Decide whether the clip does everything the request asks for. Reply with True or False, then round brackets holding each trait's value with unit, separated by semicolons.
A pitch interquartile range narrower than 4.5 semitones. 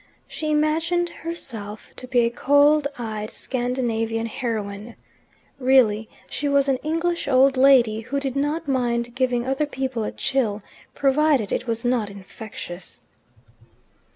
True (3.9 semitones)